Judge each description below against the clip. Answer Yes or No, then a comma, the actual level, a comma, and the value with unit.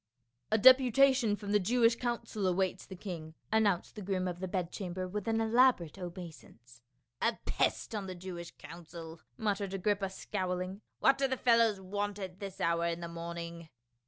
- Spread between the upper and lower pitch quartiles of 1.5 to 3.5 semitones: No, average, 4.0 semitones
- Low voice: No, high, 190 Hz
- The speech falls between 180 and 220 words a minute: Yes, average, 185 wpm